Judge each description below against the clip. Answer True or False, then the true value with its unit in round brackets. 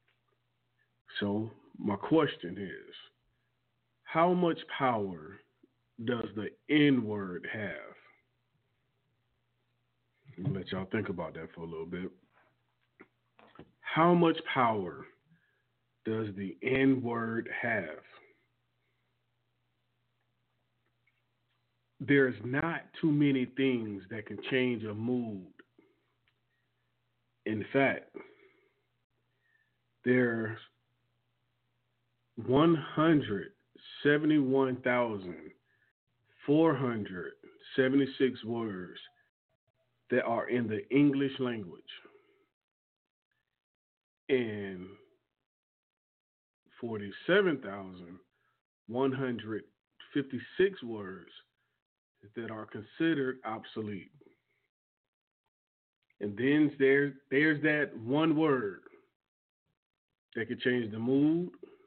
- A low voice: True (125 Hz)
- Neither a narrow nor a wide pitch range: True (3.6 semitones)